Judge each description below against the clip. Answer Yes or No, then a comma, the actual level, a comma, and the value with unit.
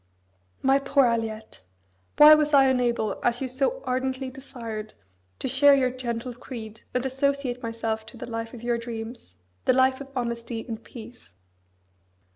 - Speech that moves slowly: No, average, 155 wpm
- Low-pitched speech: No, high, 245 Hz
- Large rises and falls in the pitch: No, average, 2.7 semitones